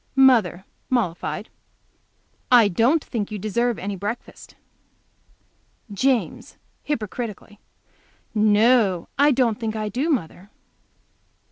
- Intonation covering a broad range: No, average, 3.3 semitones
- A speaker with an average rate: No, slow, 95 wpm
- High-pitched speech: Yes, high, 220 Hz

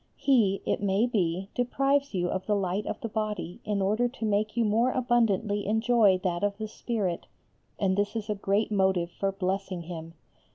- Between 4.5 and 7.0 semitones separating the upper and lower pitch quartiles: No, average, 2.8 semitones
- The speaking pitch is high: Yes, high, 205 Hz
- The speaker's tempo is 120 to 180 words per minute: No, average, 190 wpm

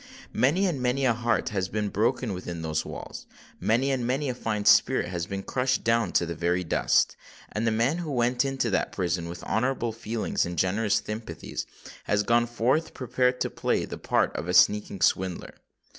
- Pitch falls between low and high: No, low, 115 Hz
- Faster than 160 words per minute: Yes, average, 190 wpm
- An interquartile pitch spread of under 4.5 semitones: No, average, 5.1 semitones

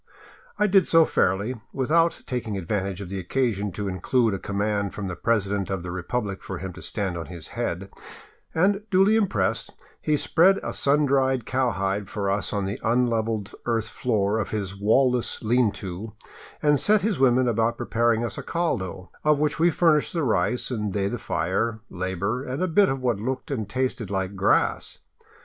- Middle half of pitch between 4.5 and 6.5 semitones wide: Yes, average, 5.2 semitones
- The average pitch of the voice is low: Yes, low, 110 Hz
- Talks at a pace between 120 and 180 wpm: No, average, 190 wpm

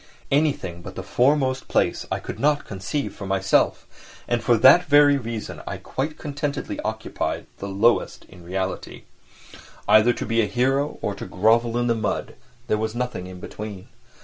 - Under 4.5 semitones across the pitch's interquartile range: No, wide, 5.6 semitones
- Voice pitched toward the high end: No, low, 115 Hz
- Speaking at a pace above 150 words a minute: Yes, average, 160 wpm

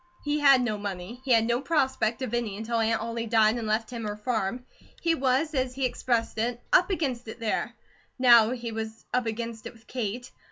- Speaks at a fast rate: Yes, fast, 210 wpm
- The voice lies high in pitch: Yes, high, 235 Hz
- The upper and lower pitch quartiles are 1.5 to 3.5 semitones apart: Yes, narrow, 2.4 semitones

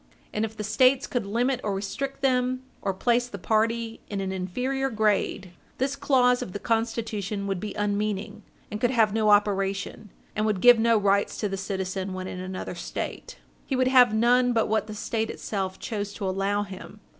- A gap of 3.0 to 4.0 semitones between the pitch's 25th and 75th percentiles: Yes, average, 3.5 semitones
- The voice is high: Yes, high, 215 Hz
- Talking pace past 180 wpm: Yes, average, 190 wpm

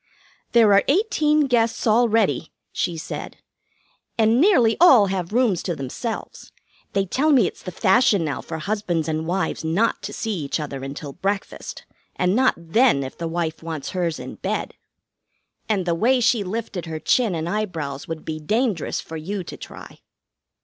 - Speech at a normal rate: Yes, average, 170 wpm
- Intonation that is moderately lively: No, wide, 6.0 semitones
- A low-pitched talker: No, high, 195 Hz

